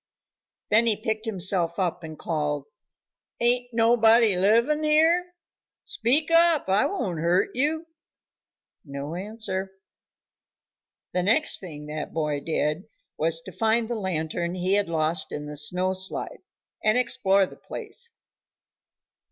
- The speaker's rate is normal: No, slow, 125 wpm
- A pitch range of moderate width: No, wide, 6.1 semitones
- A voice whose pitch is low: No, high, 190 Hz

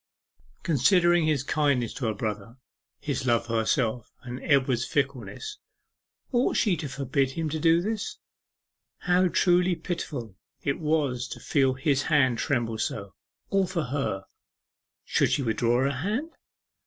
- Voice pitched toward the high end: No, medium, 140 Hz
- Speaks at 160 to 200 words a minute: No, average, 140 wpm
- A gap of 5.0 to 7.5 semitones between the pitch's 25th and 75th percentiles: Yes, wide, 5.5 semitones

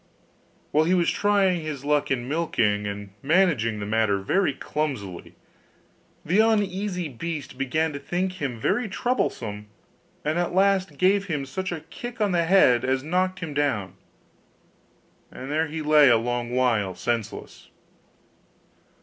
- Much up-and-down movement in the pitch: Yes, wide, 7.1 semitones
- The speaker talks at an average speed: Yes, average, 145 wpm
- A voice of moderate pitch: Yes, medium, 150 Hz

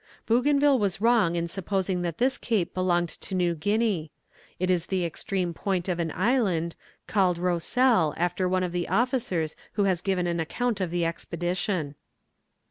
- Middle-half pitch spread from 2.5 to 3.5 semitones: Yes, average, 3.2 semitones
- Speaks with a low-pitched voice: No, medium, 180 Hz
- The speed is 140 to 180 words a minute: Yes, average, 165 wpm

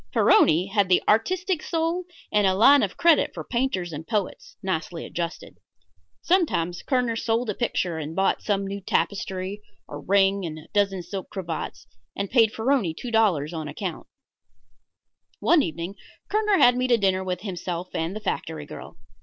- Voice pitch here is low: No, high, 195 Hz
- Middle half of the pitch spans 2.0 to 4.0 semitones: No, average, 5.1 semitones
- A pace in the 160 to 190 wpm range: Yes, average, 165 wpm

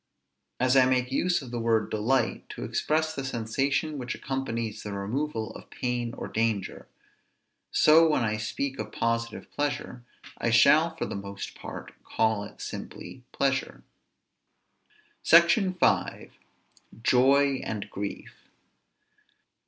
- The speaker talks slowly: Yes, slow, 130 wpm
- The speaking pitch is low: Yes, low, 125 Hz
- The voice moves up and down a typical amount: Yes, average, 4.2 semitones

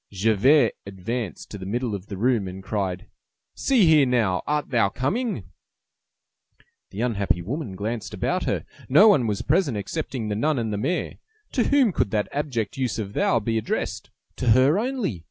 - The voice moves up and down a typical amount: No, wide, 6.3 semitones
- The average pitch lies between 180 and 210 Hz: No, low, 115 Hz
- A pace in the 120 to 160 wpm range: No, average, 175 wpm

